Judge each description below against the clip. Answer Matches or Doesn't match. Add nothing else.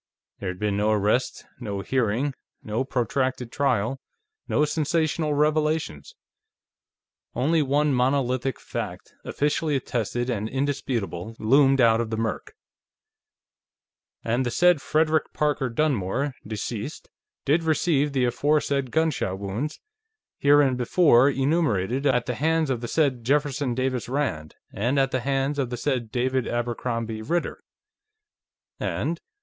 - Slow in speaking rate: Matches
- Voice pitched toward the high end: Doesn't match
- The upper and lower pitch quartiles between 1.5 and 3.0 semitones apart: Doesn't match